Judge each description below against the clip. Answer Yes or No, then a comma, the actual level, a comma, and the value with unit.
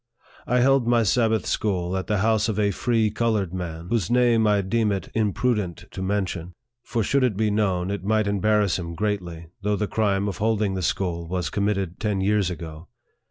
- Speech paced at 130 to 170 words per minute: No, average, 200 wpm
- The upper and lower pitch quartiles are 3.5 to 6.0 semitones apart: No, average, 3.1 semitones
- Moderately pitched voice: No, low, 100 Hz